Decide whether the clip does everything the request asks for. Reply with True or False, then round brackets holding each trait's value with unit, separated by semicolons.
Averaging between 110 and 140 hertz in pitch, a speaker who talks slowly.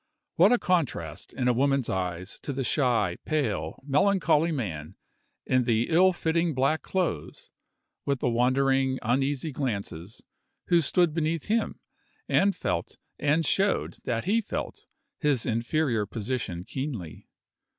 True (135 Hz; 130 wpm)